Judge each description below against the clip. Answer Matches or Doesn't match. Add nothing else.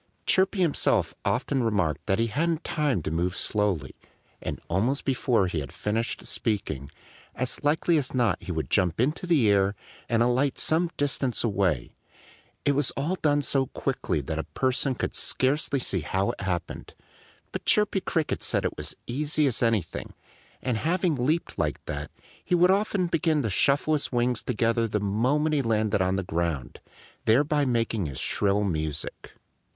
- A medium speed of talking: Matches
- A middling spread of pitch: Doesn't match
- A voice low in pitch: Matches